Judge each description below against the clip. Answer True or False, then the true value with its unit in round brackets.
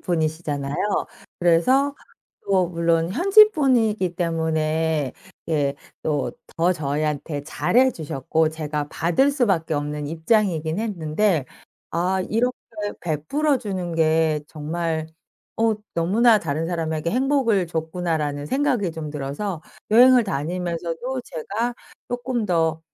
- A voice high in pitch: False (170 Hz)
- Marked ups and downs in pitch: True (5.7 semitones)